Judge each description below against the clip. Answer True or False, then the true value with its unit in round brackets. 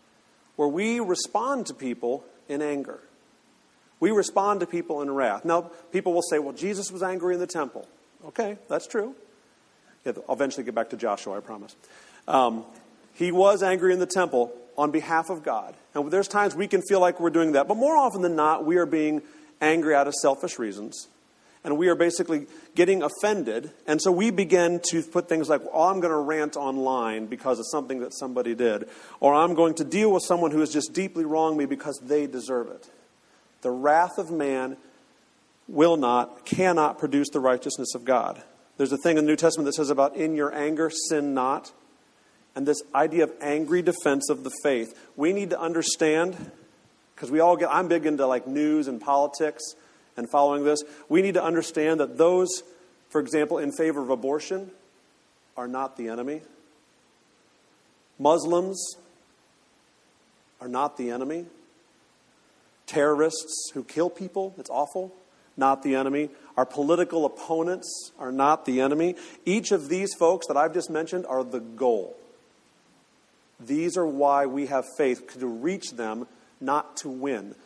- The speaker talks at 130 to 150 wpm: False (175 wpm)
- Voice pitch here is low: False (155 Hz)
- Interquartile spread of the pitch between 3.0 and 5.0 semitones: True (4.0 semitones)